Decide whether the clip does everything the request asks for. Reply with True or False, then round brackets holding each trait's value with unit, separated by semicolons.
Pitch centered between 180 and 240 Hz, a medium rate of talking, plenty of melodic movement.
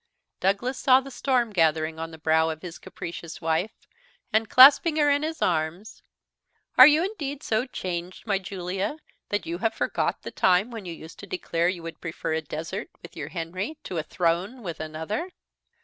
True (185 Hz; 185 wpm; 7.3 semitones)